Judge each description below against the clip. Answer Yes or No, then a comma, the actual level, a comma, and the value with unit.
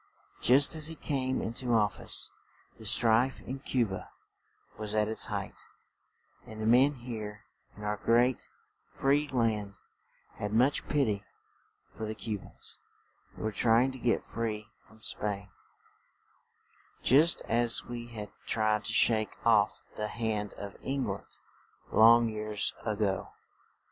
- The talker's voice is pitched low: Yes, low, 115 Hz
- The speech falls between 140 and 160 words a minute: Yes, average, 150 wpm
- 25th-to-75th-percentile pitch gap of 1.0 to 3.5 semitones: Yes, average, 2.8 semitones